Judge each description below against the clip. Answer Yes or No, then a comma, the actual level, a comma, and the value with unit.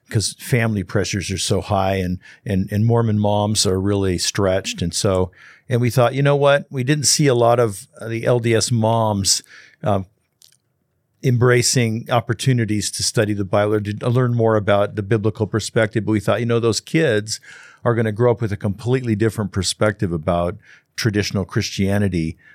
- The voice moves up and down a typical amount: Yes, average, 3.0 semitones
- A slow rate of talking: No, average, 175 wpm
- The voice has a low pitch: Yes, low, 110 Hz